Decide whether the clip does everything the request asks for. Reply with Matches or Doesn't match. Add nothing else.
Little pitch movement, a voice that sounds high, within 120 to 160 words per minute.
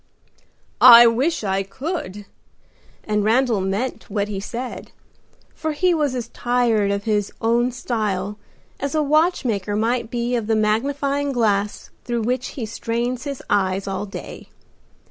Doesn't match